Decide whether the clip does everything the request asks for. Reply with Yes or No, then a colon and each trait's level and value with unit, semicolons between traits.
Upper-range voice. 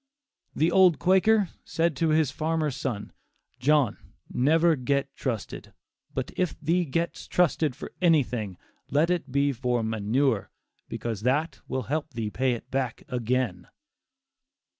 No: medium, 140 Hz